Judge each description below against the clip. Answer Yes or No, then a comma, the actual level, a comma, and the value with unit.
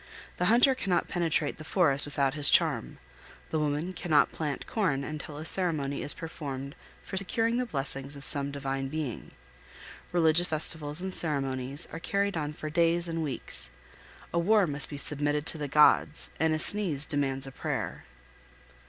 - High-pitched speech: No, medium, 150 Hz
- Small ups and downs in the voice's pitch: No, average, 3.5 semitones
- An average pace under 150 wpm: No, average, 165 wpm